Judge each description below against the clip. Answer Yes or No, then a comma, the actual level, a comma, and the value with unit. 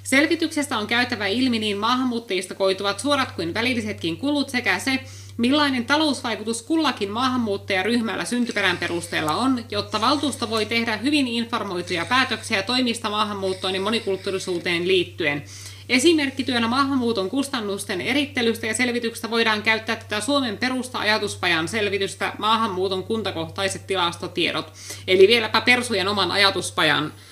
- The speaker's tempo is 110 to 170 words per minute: Yes, average, 115 wpm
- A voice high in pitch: Yes, high, 225 Hz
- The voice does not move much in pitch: No, average, 4.5 semitones